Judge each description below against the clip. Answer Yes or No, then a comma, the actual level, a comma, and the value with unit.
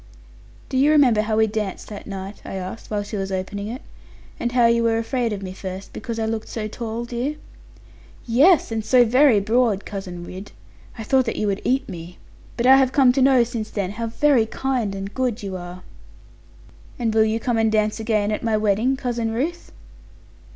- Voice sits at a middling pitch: No, high, 225 Hz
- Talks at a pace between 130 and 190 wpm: No, fast, 205 wpm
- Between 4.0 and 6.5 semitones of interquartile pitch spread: No, average, 3.3 semitones